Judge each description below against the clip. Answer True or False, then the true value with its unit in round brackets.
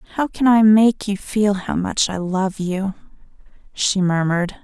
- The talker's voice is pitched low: False (200 Hz)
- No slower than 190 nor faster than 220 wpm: False (170 wpm)